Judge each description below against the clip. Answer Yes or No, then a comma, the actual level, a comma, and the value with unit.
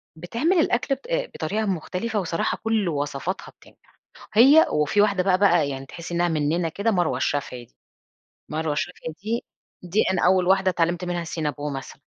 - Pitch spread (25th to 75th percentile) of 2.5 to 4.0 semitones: No, average, 4.6 semitones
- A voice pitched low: No, medium, 175 Hz